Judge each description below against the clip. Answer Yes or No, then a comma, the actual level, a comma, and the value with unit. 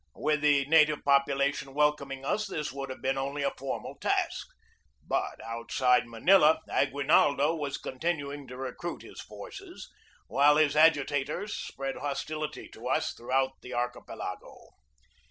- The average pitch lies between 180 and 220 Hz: No, medium, 140 Hz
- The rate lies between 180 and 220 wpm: No, slow, 135 wpm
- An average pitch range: No, narrow, 2.1 semitones